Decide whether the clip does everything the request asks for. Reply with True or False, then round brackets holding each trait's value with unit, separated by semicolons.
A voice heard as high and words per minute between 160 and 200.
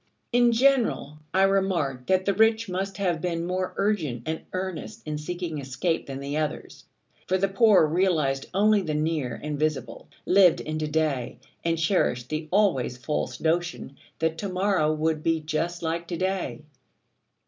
False (165 Hz; 165 wpm)